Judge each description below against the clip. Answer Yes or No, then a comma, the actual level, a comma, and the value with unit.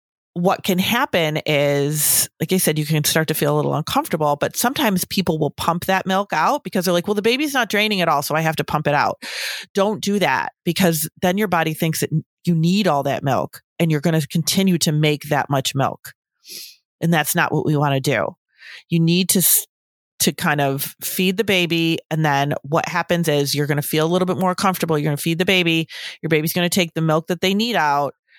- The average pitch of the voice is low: No, medium, 165 Hz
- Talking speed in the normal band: No, fast, 235 wpm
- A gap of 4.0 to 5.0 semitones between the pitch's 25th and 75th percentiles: No, average, 3.6 semitones